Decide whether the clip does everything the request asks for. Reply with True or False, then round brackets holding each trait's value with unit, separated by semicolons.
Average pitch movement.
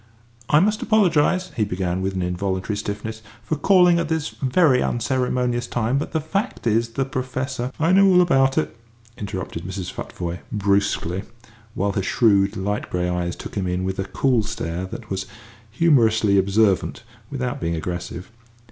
False (6.3 semitones)